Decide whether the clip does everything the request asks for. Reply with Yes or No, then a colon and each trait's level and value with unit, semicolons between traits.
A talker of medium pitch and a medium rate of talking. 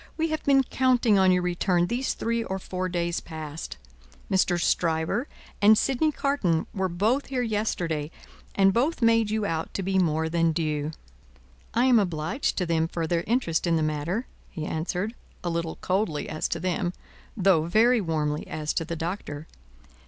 Yes: medium, 180 Hz; average, 175 wpm